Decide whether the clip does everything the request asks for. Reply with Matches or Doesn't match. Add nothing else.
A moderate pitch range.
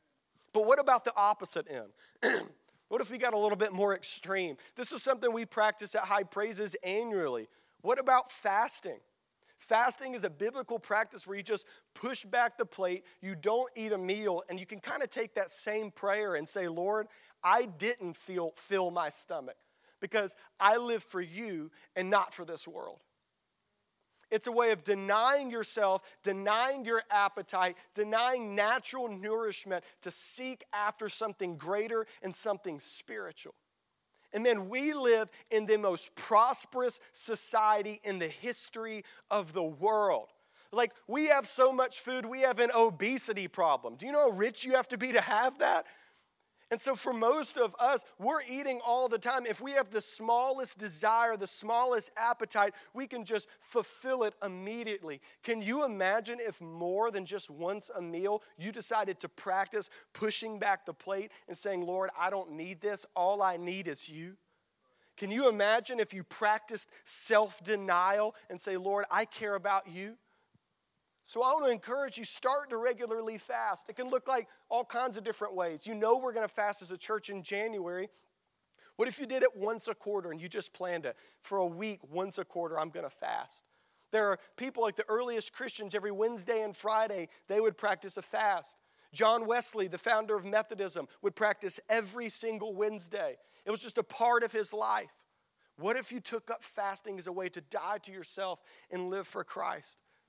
Matches